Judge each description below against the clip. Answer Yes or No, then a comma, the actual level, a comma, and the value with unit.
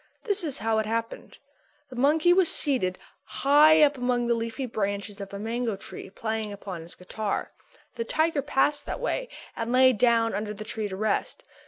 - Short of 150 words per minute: No, average, 185 wpm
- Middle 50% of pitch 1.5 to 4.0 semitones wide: No, average, 4.8 semitones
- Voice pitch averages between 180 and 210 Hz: No, high, 230 Hz